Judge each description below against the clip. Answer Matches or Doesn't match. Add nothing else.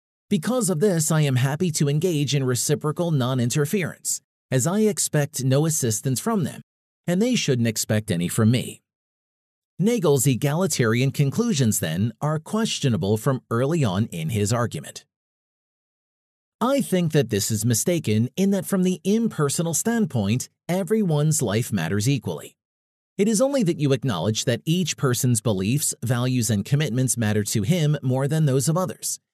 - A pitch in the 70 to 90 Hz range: Doesn't match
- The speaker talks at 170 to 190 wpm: Doesn't match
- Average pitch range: Doesn't match